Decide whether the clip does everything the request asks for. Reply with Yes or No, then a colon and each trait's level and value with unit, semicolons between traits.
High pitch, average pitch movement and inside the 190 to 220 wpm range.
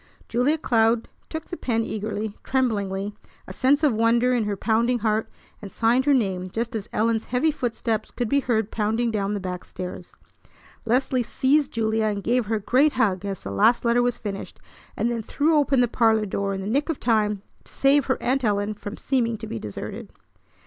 Yes: high, 225 Hz; average, 3.3 semitones; average, 200 wpm